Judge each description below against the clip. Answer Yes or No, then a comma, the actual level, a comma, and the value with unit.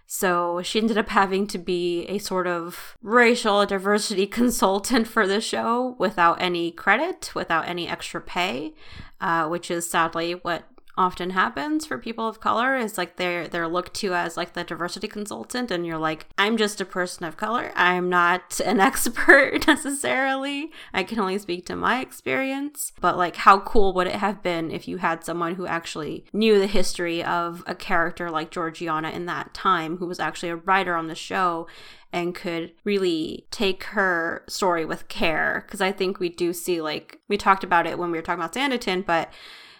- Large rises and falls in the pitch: No, average, 3.7 semitones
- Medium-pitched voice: Yes, medium, 180 Hz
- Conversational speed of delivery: Yes, average, 190 wpm